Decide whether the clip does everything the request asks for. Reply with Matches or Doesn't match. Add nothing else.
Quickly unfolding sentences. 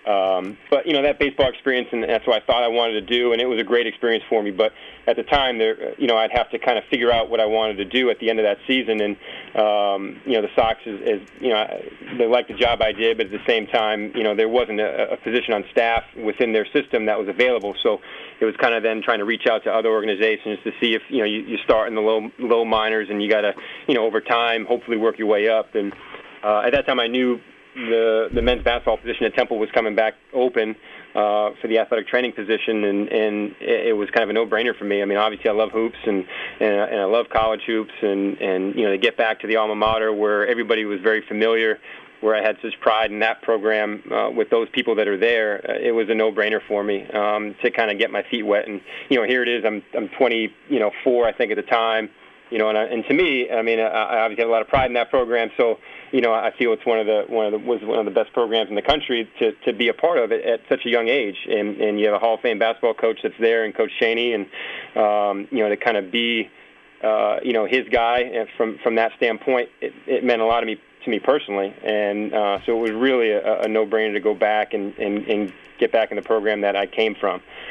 Matches